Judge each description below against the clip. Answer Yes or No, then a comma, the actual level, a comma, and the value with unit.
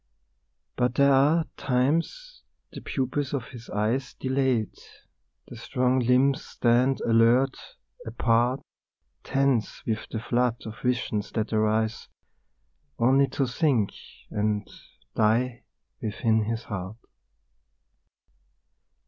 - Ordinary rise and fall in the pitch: Yes, average, 3.2 semitones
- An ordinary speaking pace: No, slow, 100 wpm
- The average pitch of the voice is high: No, low, 125 Hz